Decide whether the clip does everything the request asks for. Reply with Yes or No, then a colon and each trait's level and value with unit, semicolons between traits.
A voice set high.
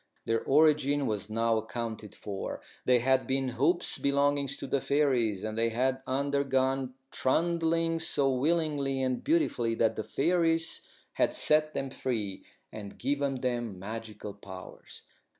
No: low, 130 Hz